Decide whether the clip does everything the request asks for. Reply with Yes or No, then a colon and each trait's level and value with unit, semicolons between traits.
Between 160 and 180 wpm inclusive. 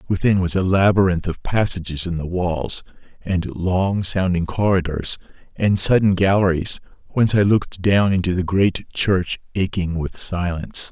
No: average, 150 wpm